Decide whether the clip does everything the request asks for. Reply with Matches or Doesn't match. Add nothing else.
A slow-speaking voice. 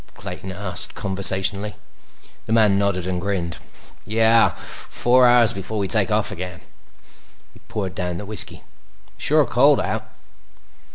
Matches